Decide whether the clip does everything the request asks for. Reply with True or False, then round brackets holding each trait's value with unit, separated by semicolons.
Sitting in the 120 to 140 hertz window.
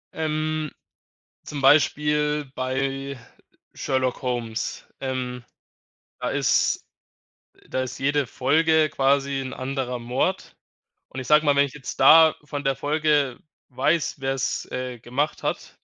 True (135 Hz)